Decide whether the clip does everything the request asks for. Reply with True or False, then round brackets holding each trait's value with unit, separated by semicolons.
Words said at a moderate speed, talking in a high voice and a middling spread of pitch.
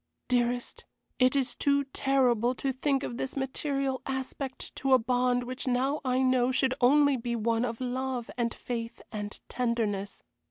False (160 wpm; 255 Hz; 1.8 semitones)